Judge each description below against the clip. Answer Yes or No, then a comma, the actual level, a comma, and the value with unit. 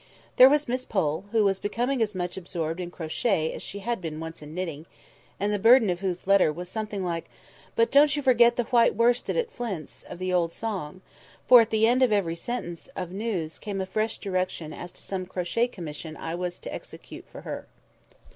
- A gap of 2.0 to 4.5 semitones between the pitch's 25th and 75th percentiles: No, average, 5.1 semitones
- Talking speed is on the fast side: Yes, fast, 215 wpm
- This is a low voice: No, high, 190 Hz